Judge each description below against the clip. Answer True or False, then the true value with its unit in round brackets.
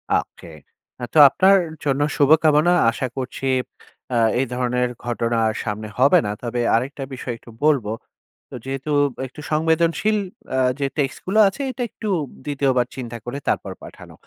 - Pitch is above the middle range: False (135 Hz)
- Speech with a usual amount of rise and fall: True (3.8 semitones)